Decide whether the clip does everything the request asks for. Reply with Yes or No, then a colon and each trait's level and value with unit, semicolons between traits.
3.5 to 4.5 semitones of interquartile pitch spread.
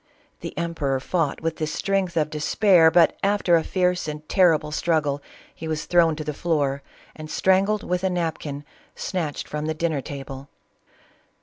No: average, 2.9 semitones